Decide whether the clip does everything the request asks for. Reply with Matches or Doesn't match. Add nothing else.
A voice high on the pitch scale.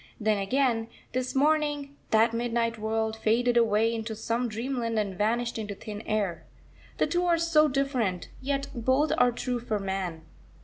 Matches